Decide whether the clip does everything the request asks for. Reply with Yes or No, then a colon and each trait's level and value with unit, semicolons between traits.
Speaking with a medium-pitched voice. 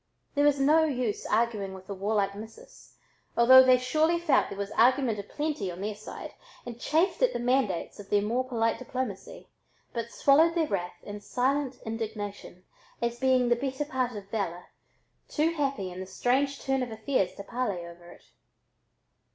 No: high, 240 Hz